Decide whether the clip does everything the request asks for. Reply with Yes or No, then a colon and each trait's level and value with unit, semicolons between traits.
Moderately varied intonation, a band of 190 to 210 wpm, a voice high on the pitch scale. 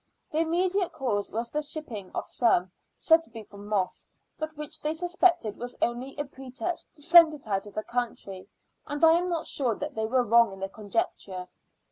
No: wide, 6.6 semitones; average, 200 wpm; very high, 255 Hz